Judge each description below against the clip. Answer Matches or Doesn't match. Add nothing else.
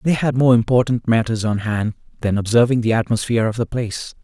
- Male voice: Matches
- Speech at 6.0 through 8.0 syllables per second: Matches